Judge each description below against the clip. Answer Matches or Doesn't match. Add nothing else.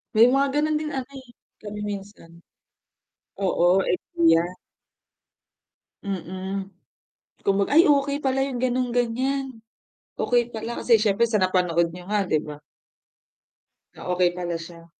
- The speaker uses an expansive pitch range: Matches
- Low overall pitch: Doesn't match